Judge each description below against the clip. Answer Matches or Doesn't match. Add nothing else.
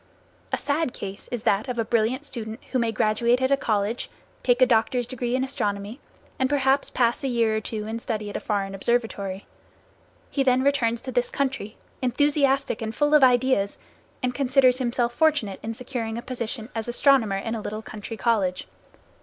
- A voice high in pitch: Matches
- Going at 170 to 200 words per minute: Matches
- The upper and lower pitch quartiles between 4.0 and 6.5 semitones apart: Doesn't match